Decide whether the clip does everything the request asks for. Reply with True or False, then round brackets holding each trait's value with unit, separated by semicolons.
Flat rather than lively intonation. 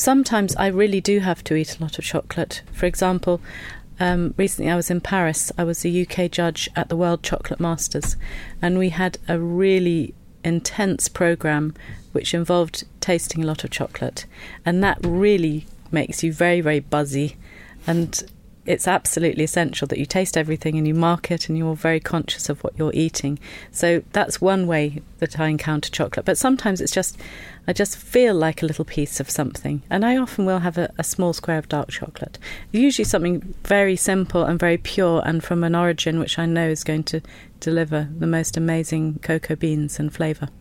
True (2.3 semitones)